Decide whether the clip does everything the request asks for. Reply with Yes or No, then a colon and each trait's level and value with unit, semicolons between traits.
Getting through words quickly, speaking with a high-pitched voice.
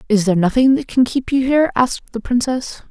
Yes: fast, 225 wpm; high, 245 Hz